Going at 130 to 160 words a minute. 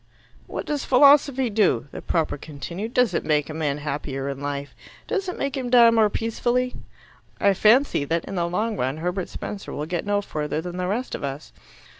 No: average, 200 wpm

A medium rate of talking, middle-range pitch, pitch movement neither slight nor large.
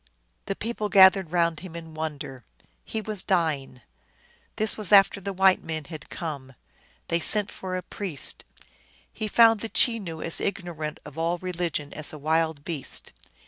Yes: average, 160 wpm; medium, 170 Hz; average, 4.0 semitones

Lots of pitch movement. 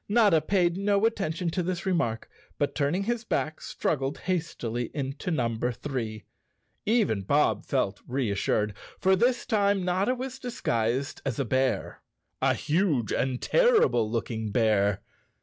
Yes: wide, 8.9 semitones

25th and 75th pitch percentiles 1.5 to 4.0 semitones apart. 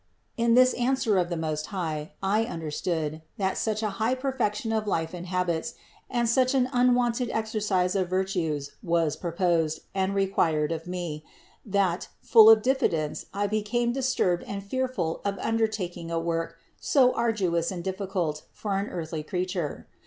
No: average, 5.0 semitones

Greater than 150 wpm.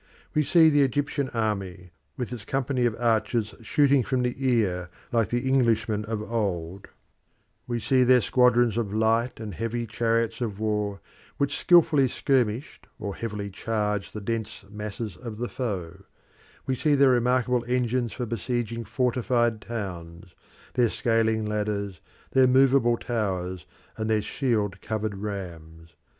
No: average, 140 wpm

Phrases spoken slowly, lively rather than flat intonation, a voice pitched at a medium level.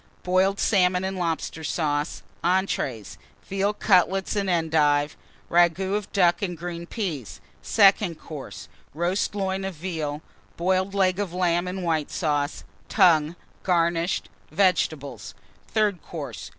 No: slow, 125 wpm; average, 3.2 semitones; medium, 175 Hz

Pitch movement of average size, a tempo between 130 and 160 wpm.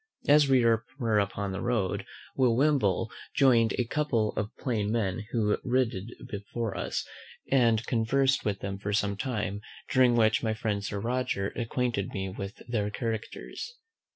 Yes: average, 3.5 semitones; average, 155 wpm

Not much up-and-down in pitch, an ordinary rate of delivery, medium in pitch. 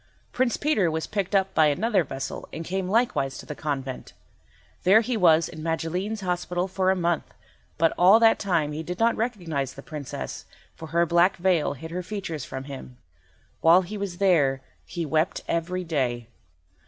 No: average, 3.7 semitones; average, 180 wpm; medium, 175 Hz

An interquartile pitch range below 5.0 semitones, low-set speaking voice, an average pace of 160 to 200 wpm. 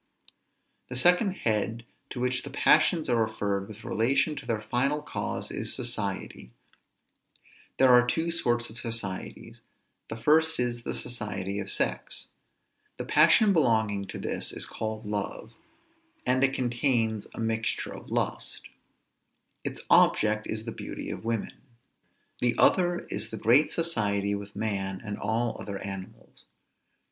No: average, 3.6 semitones; low, 115 Hz; average, 140 wpm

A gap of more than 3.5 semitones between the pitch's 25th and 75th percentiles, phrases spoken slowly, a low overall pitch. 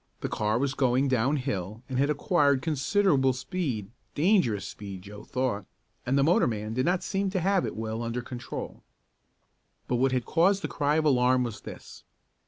No: average, 5.1 semitones; average, 180 wpm; low, 130 Hz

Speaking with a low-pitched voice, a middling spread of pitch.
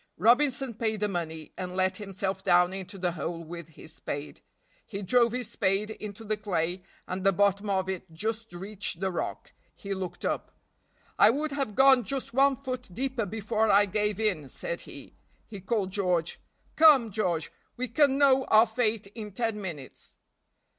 No: high, 205 Hz; average, 4.0 semitones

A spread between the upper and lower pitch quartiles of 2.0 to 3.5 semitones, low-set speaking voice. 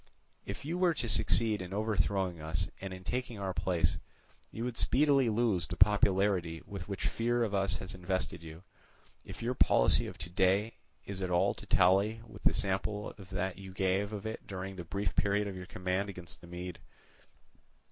Yes: narrow, 2.6 semitones; very low, 95 Hz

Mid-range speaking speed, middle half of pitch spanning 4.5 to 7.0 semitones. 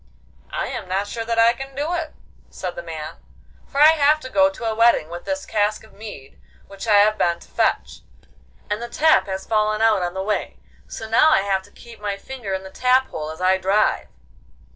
No: fast, 225 wpm; average, 4.9 semitones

